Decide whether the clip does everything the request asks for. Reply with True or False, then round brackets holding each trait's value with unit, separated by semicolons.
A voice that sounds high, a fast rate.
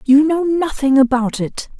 False (280 Hz; 165 wpm)